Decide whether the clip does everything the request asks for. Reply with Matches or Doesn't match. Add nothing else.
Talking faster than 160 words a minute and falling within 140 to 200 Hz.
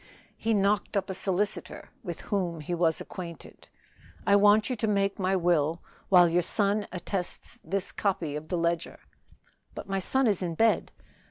Matches